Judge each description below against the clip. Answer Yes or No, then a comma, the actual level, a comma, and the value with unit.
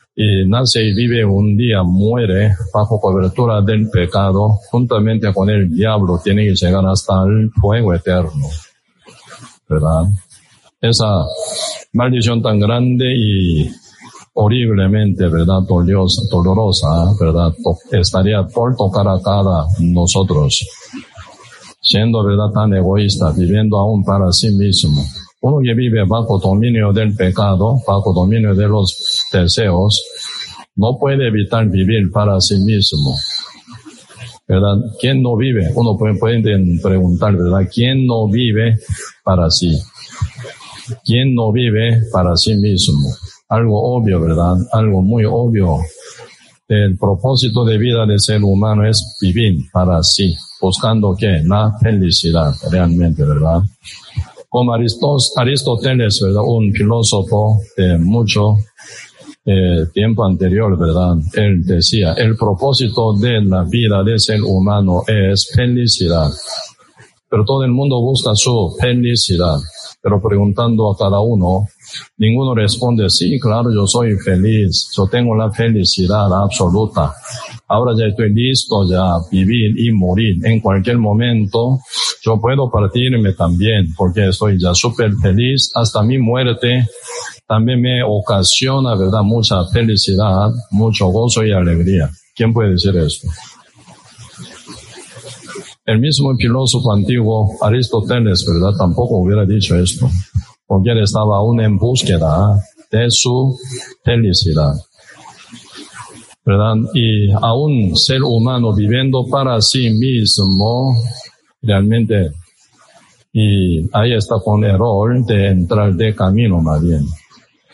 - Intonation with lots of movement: No, average, 3.5 semitones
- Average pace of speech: No, slow, 120 wpm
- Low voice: Yes, low, 105 Hz